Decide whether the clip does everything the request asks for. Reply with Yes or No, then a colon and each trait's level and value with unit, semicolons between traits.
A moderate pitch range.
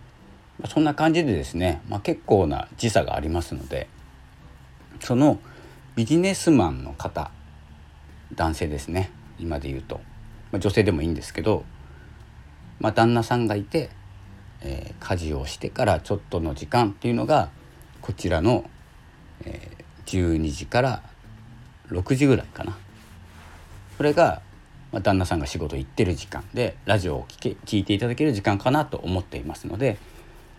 No: wide, 6.2 semitones